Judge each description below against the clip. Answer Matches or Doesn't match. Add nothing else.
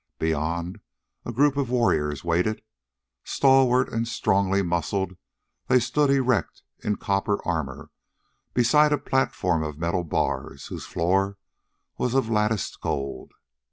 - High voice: Doesn't match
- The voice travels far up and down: Matches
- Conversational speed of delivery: Doesn't match